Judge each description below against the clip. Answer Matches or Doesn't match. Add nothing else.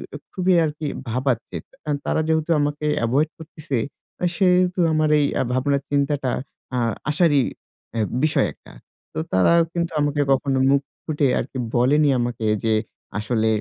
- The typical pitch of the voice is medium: Matches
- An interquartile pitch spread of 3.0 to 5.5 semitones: Matches